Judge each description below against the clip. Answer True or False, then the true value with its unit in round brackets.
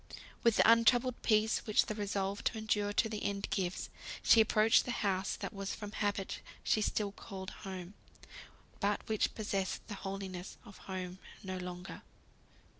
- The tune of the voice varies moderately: False (2.1 semitones)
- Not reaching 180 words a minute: True (155 wpm)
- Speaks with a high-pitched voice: True (205 Hz)